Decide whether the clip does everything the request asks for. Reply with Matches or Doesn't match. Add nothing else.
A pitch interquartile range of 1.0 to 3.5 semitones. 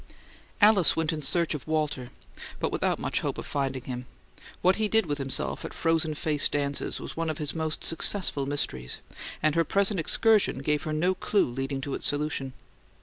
Matches